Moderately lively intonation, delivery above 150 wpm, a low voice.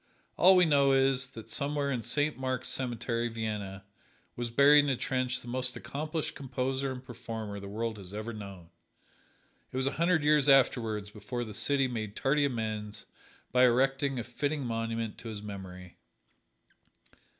Yes: average, 3.9 semitones; average, 160 wpm; low, 125 Hz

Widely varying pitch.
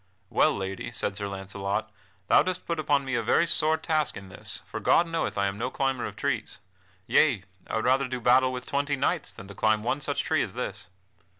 Yes: wide, 5.9 semitones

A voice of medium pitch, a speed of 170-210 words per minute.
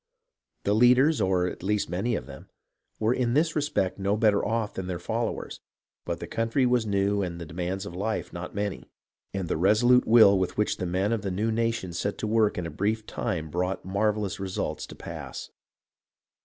No: low, 100 Hz; average, 195 wpm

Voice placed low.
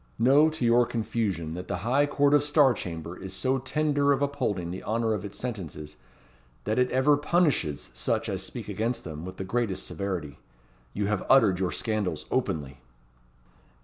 Yes: low, 110 Hz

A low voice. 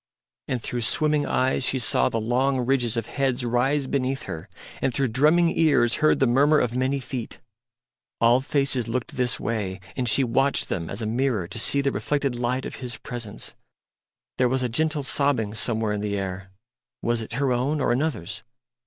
Yes: low, 125 Hz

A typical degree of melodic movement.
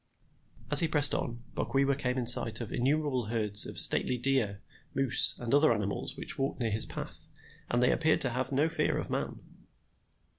Yes: average, 3.1 semitones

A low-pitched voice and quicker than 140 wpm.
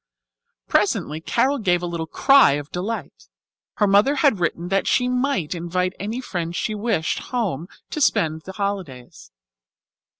No: high, 190 Hz; average, 160 wpm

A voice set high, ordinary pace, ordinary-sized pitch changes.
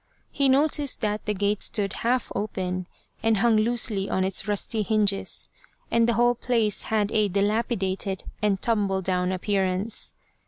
Yes: high, 210 Hz; average, 150 wpm; average, 3.0 semitones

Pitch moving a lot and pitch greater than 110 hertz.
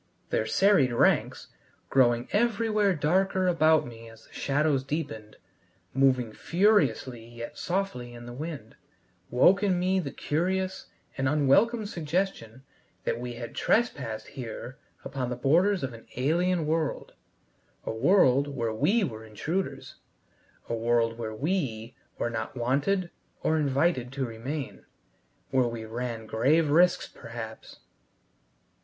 Yes: wide, 7.0 semitones; low, 135 Hz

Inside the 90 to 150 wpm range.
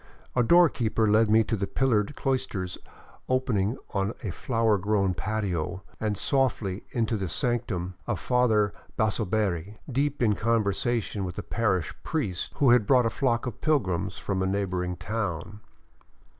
Yes: average, 145 wpm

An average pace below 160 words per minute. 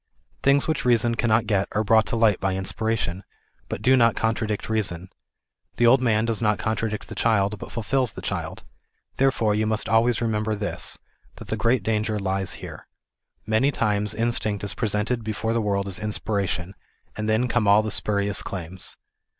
No: average, 190 wpm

